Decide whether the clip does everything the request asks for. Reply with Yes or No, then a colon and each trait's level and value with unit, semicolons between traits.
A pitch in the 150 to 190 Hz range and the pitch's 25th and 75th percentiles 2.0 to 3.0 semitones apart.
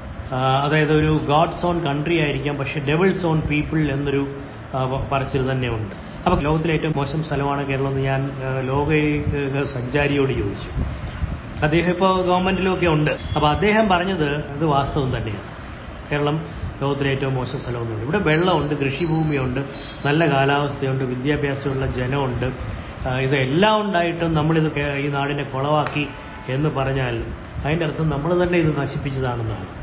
No: medium, 140 Hz; narrow, 2.5 semitones